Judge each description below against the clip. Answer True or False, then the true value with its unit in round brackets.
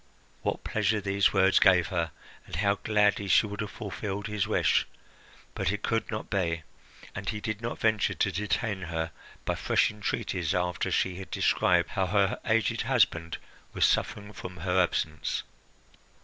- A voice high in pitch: False (100 Hz)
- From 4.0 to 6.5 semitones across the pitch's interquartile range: False (2.8 semitones)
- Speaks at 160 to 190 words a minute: True (165 wpm)